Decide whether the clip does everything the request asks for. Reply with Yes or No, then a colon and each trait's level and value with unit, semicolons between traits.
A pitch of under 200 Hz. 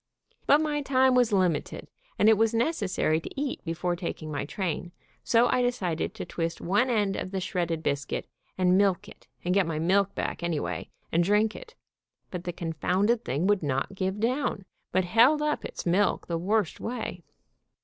Yes: high, 190 Hz